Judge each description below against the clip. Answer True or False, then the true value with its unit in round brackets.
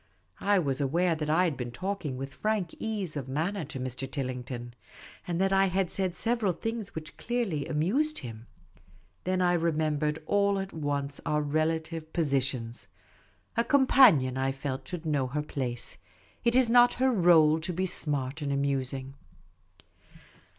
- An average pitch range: False (5.9 semitones)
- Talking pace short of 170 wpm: True (155 wpm)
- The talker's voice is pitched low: False (155 Hz)